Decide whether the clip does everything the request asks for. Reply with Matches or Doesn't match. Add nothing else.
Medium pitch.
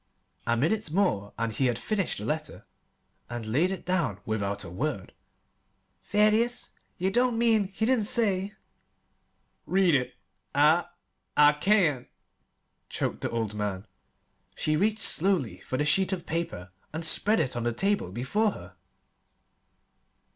Matches